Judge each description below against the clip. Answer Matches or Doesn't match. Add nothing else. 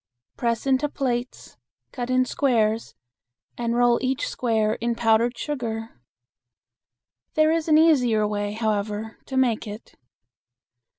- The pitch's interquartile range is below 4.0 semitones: Matches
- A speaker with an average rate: Doesn't match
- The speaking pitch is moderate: Doesn't match